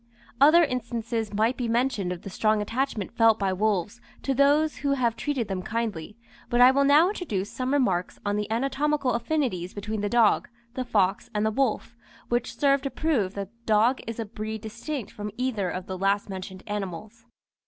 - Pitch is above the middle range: Yes, high, 225 Hz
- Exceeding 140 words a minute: Yes, average, 195 wpm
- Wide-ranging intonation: No, average, 4.2 semitones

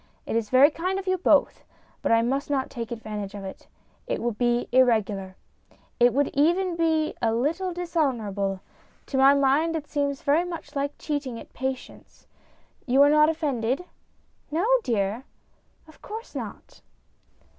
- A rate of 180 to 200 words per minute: No, average, 170 wpm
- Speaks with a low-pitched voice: No, very high, 275 Hz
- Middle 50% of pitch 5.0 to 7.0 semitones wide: Yes, wide, 5.5 semitones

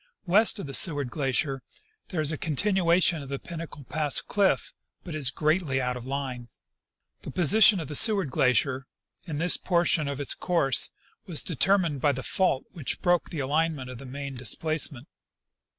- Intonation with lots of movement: No, average, 4.3 semitones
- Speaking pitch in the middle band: Yes, medium, 150 Hz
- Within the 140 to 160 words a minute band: No, average, 180 wpm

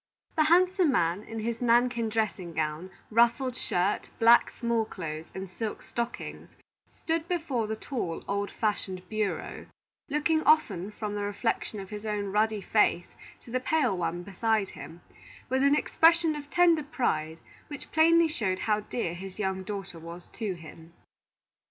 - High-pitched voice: Yes, high, 215 Hz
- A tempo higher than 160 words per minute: No, average, 155 wpm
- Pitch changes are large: Yes, wide, 5.7 semitones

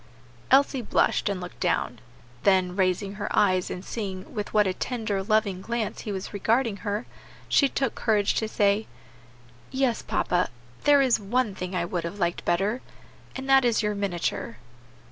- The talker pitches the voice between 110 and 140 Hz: No, high, 205 Hz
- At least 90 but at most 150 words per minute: No, average, 165 wpm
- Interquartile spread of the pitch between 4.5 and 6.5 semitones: No, average, 3.7 semitones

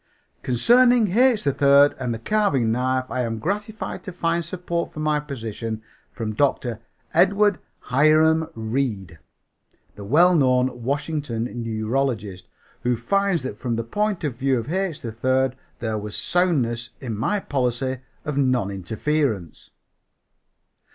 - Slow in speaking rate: Yes, slow, 130 wpm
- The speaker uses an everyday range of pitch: No, wide, 6.4 semitones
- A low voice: Yes, low, 130 Hz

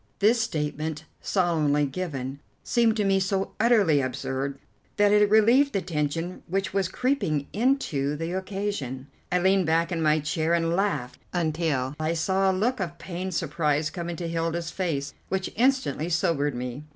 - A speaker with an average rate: Yes, average, 160 wpm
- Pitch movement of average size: Yes, average, 4.5 semitones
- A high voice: No, medium, 170 Hz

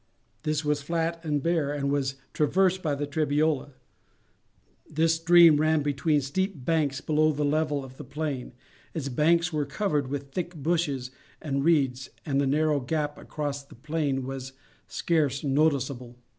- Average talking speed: Yes, average, 155 wpm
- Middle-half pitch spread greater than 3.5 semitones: No, narrow, 2.4 semitones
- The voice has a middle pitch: Yes, medium, 150 Hz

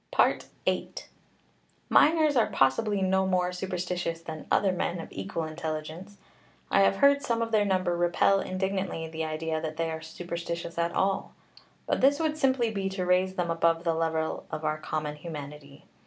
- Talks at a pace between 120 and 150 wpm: No, average, 170 wpm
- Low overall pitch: No, medium, 175 Hz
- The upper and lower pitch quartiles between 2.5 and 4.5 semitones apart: Yes, average, 3.3 semitones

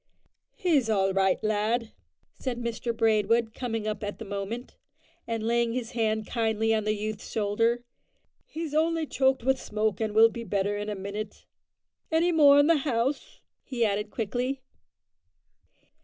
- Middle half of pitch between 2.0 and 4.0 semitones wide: Yes, average, 2.9 semitones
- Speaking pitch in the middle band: No, high, 225 Hz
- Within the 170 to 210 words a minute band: No, average, 155 wpm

